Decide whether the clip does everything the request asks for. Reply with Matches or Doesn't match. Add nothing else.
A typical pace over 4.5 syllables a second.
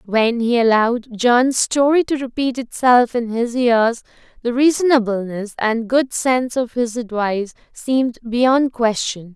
Doesn't match